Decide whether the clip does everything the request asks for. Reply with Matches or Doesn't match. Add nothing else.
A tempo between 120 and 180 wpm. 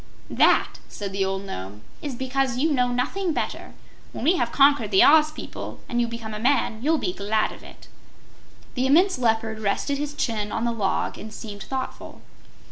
Doesn't match